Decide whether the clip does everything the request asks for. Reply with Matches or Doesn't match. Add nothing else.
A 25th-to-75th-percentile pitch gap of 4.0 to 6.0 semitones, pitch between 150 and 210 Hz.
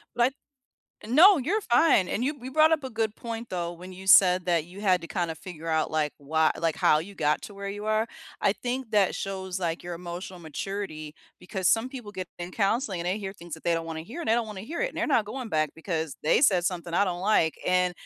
Matches